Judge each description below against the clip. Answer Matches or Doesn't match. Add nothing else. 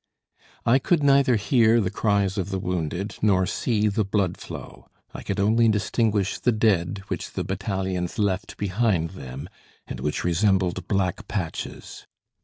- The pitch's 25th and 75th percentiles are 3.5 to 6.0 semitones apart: Doesn't match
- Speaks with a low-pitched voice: Matches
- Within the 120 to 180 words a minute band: Matches